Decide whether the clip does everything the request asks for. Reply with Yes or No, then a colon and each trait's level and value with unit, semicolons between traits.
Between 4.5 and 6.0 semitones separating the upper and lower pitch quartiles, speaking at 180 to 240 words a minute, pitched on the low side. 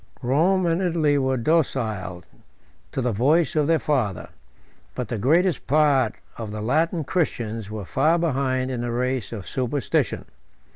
No: average, 5.2 semitones; average, 150 wpm; low, 130 Hz